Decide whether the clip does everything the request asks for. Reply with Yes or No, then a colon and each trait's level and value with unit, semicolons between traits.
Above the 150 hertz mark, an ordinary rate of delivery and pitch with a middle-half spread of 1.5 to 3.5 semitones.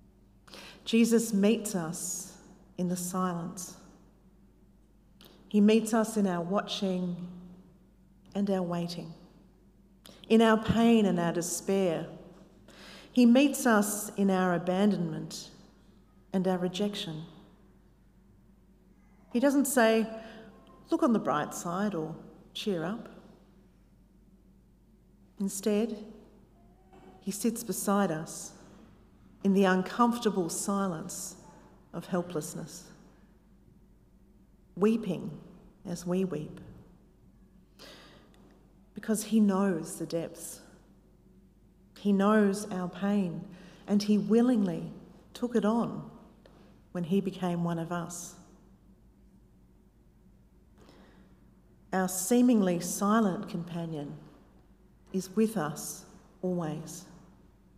No: high, 190 Hz; slow, 90 wpm; average, 2.8 semitones